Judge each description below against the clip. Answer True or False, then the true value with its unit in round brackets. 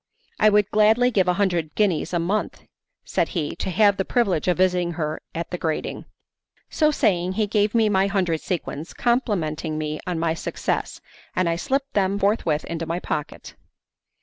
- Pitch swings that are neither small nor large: True (3.9 semitones)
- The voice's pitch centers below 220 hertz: True (185 Hz)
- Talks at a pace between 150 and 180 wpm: True (175 wpm)